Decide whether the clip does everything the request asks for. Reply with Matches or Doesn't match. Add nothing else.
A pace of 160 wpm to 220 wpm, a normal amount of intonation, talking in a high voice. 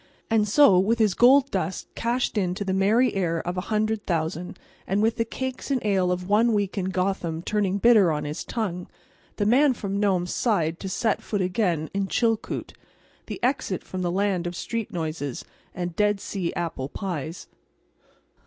Matches